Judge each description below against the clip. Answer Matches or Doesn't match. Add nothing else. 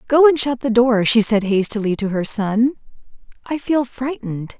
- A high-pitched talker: Matches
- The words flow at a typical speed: Matches